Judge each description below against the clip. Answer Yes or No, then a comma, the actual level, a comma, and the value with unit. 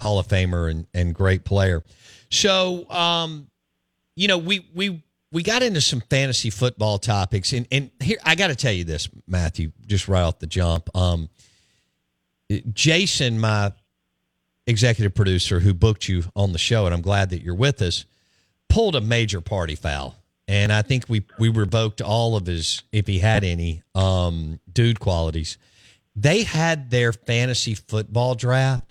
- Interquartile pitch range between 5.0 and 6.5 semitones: Yes, wide, 5.6 semitones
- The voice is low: Yes, low, 105 Hz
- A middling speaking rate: Yes, average, 165 wpm